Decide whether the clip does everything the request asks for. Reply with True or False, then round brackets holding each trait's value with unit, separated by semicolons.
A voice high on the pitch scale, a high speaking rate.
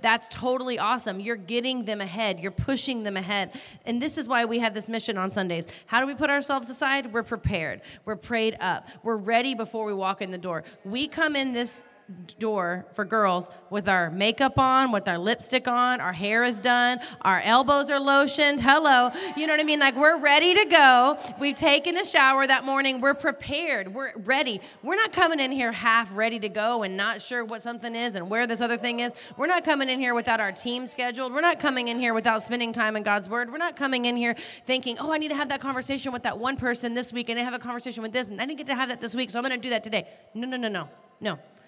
True (240 Hz; 250 wpm)